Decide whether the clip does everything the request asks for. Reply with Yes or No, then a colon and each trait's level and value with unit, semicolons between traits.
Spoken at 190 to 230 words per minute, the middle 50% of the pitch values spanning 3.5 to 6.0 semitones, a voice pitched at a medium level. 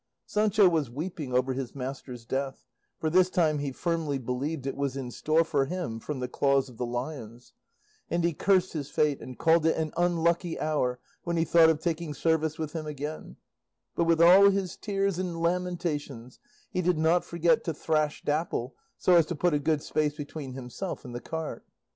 Yes: average, 195 wpm; average, 3.9 semitones; medium, 155 Hz